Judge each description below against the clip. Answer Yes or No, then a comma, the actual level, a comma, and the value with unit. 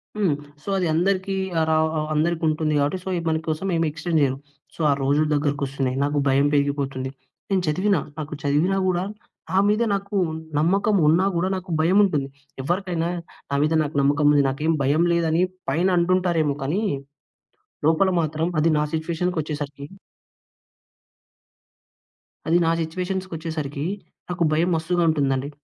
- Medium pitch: Yes, medium, 160 Hz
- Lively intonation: No, average, 3.5 semitones